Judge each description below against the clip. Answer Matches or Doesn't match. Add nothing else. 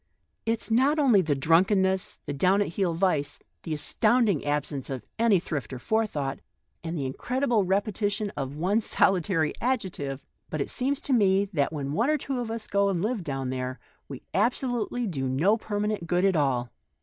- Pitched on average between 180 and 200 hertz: Matches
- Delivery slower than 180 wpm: Doesn't match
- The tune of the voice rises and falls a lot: Matches